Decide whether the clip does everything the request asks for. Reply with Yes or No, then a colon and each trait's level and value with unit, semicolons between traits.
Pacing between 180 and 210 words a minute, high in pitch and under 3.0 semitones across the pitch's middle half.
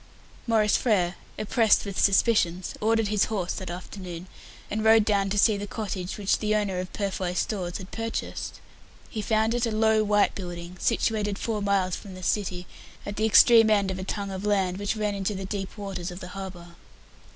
Yes: average, 195 wpm; high, 200 Hz; narrow, 2.5 semitones